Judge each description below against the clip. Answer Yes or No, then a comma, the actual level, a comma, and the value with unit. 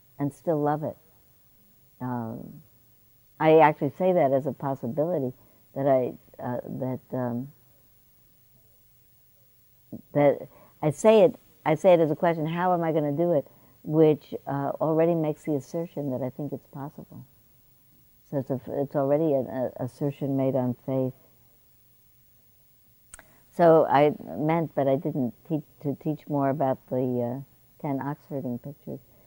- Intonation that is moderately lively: Yes, average, 3.6 semitones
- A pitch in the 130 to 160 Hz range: Yes, low, 135 Hz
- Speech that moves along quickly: No, average, 150 wpm